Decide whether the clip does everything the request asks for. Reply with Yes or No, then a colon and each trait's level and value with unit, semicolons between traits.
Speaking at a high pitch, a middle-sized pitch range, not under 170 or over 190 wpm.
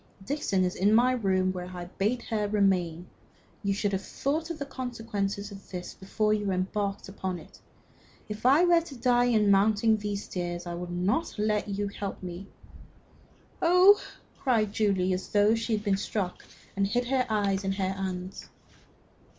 Yes: high, 205 Hz; average, 3.2 semitones; average, 175 wpm